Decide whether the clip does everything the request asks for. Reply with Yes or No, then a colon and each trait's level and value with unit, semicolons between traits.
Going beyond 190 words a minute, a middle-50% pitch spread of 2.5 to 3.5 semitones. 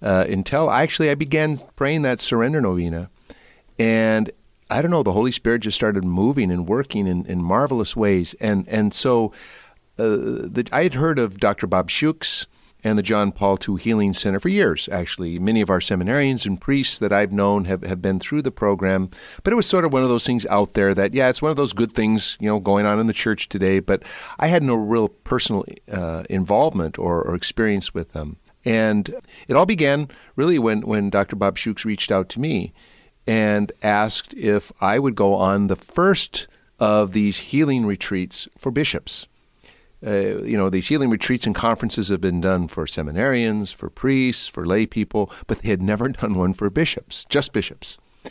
No: average, 200 wpm; average, 3.9 semitones